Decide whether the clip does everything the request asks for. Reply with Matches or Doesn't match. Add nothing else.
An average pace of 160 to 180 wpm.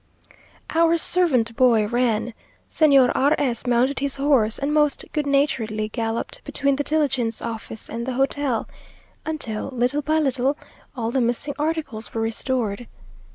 Doesn't match